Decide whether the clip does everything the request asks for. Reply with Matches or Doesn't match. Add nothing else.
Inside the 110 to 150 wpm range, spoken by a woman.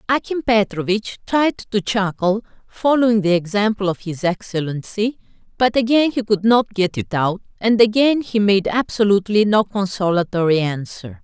Matches